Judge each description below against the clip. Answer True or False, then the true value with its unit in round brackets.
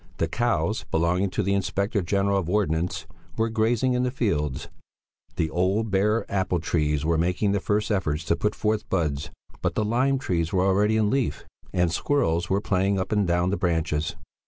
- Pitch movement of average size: True (4.0 semitones)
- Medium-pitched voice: False (95 Hz)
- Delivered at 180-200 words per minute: True (185 wpm)